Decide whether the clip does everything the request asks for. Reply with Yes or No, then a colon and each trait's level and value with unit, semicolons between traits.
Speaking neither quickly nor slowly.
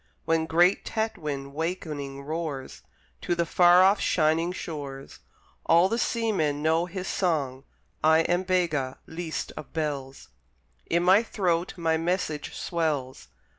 No: slow, 130 wpm